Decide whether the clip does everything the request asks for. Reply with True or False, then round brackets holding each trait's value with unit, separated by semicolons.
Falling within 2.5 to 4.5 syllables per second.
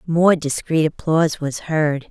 True (4.1 syllables/s)